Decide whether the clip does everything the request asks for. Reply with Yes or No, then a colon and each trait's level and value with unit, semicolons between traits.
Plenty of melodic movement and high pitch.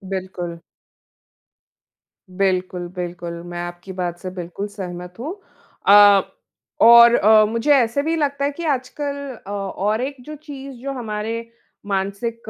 Yes: wide, 6.2 semitones; high, 210 Hz